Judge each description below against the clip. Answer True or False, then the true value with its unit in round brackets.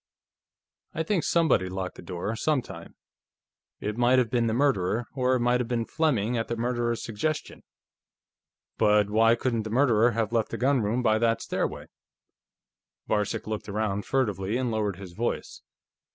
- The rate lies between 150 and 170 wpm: True (160 wpm)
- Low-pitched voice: True (115 Hz)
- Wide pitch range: False (2.9 semitones)